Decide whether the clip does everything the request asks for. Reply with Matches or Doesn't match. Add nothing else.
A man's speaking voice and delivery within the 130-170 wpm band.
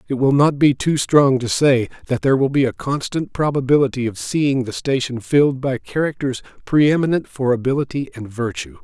Doesn't match